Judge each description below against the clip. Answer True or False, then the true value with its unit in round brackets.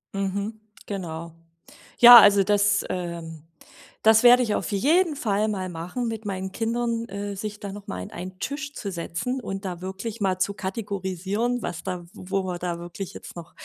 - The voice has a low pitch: False (200 Hz)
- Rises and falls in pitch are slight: False (3.3 semitones)